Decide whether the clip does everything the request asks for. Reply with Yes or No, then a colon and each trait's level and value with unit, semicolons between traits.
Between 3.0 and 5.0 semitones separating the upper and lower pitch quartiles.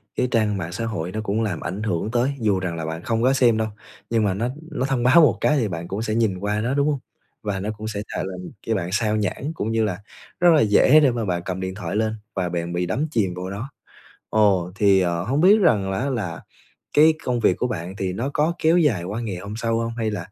Yes: average, 4.3 semitones